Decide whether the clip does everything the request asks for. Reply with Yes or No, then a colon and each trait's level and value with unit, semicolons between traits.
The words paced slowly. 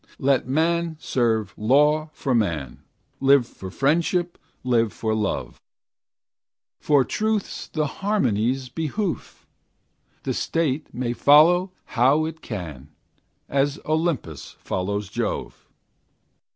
Yes: slow, 100 wpm